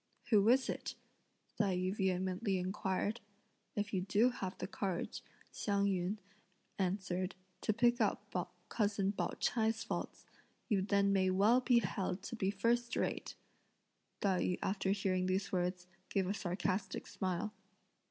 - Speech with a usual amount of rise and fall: No, narrow, 2.3 semitones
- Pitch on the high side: Yes, high, 195 Hz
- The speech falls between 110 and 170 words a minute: Yes, average, 140 wpm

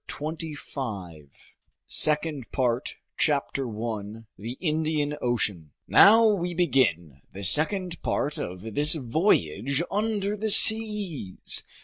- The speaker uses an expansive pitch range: Yes, wide, 7.8 semitones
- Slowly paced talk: Yes, slow, 120 wpm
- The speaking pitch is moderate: Yes, medium, 145 Hz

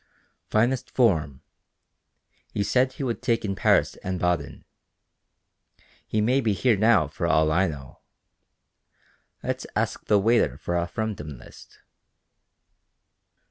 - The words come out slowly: Yes, slow, 120 wpm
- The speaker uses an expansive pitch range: Yes, wide, 6.0 semitones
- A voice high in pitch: No, low, 100 Hz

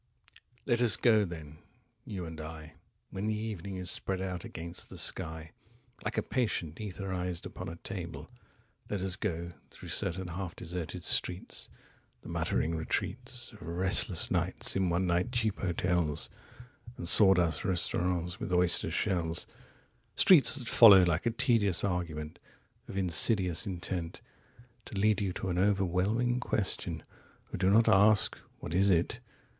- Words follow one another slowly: Yes, slow, 130 wpm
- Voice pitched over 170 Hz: No, very low, 95 Hz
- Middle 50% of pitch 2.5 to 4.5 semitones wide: Yes, average, 3.8 semitones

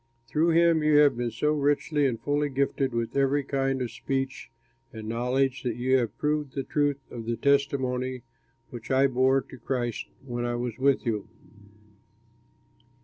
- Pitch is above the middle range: No, low, 135 Hz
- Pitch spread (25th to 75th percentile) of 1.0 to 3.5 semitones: Yes, average, 2.7 semitones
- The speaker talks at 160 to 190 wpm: Yes, average, 165 wpm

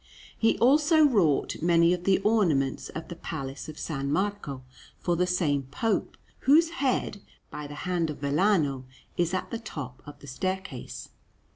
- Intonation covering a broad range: Yes, wide, 6.1 semitones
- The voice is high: No, medium, 175 Hz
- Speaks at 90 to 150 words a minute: No, average, 160 wpm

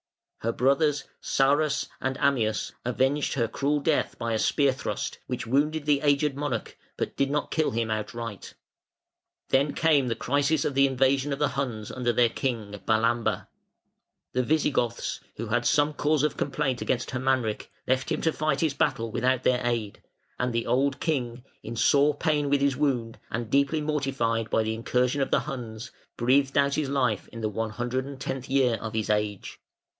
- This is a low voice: Yes, low, 130 Hz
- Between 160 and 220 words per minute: Yes, average, 180 wpm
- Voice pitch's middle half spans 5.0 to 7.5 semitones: No, average, 3.4 semitones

